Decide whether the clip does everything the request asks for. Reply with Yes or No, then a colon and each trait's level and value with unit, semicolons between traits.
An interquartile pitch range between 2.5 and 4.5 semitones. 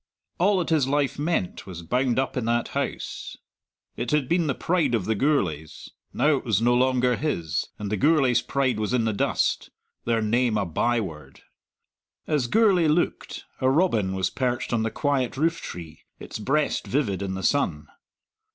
No: wide, 5.6 semitones